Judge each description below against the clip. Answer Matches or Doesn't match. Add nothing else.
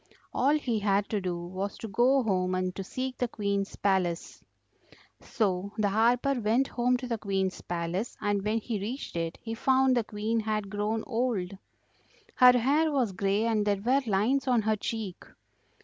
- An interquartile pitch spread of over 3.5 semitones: Matches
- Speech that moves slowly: Doesn't match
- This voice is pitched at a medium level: Doesn't match